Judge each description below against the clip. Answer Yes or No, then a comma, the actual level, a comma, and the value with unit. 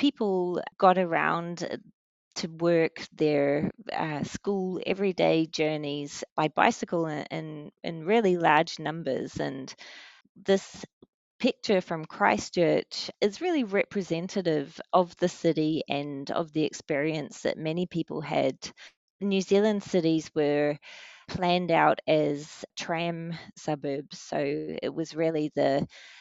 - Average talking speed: No, slow, 115 wpm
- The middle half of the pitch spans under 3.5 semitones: No, average, 4.1 semitones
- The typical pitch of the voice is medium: Yes, medium, 170 Hz